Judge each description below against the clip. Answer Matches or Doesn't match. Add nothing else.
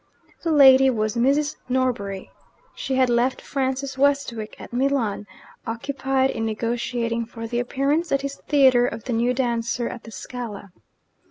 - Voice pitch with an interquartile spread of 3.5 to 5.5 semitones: Doesn't match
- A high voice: Matches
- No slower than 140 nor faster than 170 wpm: Matches